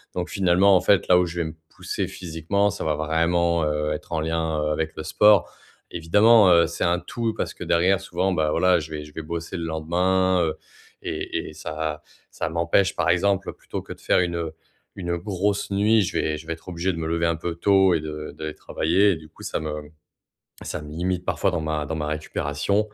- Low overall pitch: Yes, very low, 85 Hz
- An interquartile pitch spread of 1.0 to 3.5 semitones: Yes, average, 2.9 semitones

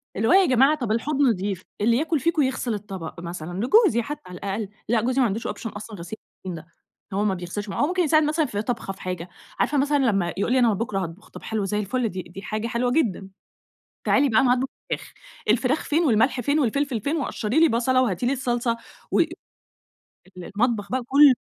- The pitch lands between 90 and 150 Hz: No, high, 235 Hz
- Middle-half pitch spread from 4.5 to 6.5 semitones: Yes, average, 5.2 semitones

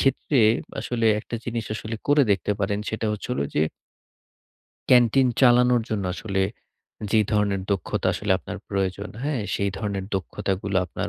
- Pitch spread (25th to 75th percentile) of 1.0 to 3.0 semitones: No, average, 3.7 semitones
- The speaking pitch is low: Yes, low, 105 Hz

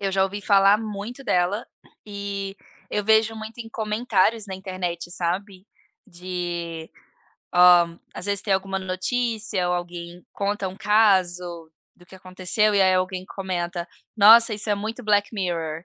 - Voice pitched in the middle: No, high, 195 Hz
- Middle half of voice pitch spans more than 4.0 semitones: No, average, 2.9 semitones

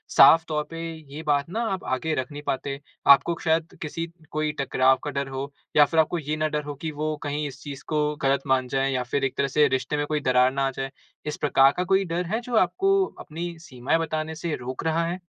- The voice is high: No, medium, 150 Hz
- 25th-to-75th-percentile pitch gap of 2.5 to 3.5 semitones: Yes, average, 2.9 semitones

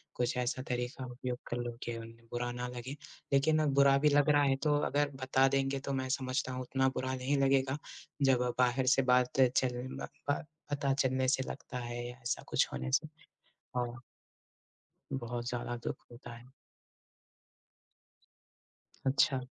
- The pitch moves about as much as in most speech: No, narrow, 1.9 semitones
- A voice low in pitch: Yes, low, 130 Hz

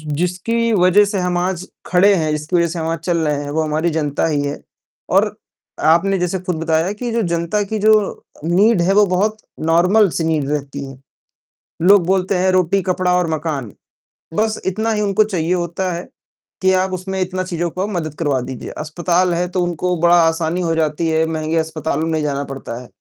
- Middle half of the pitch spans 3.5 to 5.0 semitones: No, average, 2.9 semitones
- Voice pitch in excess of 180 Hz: No, medium, 175 Hz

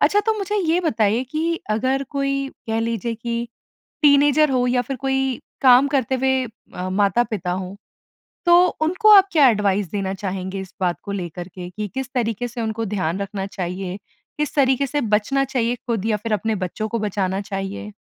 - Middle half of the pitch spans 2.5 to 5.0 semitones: No, wide, 5.5 semitones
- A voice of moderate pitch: No, high, 230 Hz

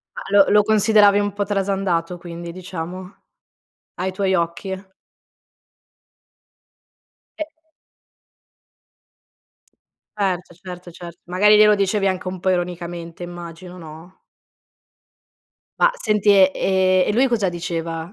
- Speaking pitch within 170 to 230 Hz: Yes, medium, 185 Hz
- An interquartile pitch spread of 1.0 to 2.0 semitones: No, narrow, 2.5 semitones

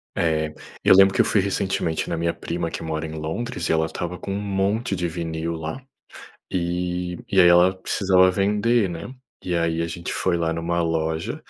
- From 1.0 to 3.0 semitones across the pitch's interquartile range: Yes, average, 2.7 semitones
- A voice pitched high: No, very low, 85 Hz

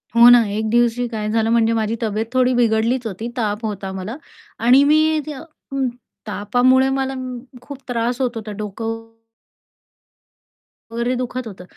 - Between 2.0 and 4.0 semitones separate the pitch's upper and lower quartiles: Yes, narrow, 2.6 semitones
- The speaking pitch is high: Yes, high, 235 Hz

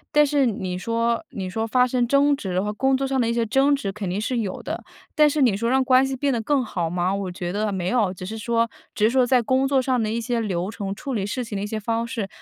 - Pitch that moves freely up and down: No, average, 4.5 semitones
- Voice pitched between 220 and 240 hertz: Yes, high, 230 Hz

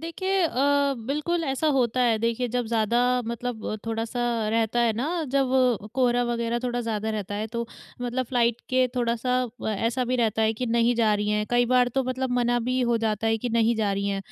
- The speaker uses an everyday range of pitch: No, narrow, 2.1 semitones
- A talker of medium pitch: No, high, 235 Hz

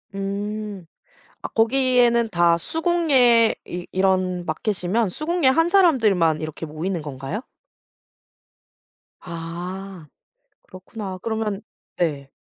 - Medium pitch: No, high, 195 Hz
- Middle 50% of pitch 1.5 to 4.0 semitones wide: No, average, 5.2 semitones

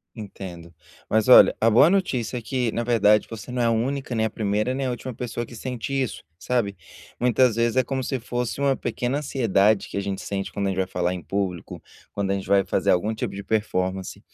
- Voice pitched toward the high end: No, low, 110 Hz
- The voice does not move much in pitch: No, average, 3.9 semitones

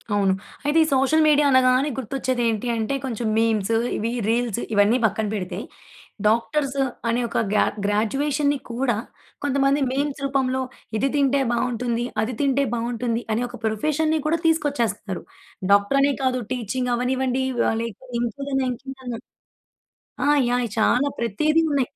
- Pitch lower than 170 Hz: No, very high, 255 Hz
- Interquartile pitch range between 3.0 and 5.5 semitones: Yes, average, 3.3 semitones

